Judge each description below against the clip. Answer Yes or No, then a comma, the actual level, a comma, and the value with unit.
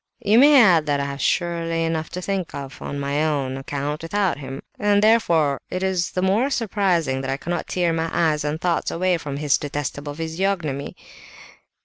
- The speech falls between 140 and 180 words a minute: No, average, 195 wpm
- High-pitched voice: No, medium, 165 Hz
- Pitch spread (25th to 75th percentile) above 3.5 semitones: Yes, average, 4.4 semitones